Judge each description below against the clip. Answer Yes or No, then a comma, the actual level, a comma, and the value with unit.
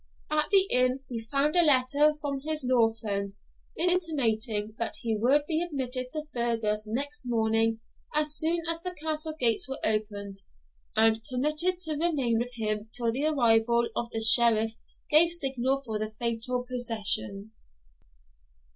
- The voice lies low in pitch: No, very high, 250 Hz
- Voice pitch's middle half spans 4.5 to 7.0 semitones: Yes, average, 5.1 semitones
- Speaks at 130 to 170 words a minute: Yes, average, 150 wpm